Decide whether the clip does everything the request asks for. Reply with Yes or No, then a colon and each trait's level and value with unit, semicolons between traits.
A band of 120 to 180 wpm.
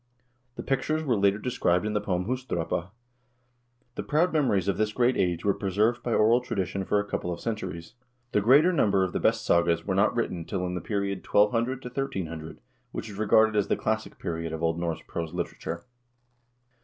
No: average, 195 wpm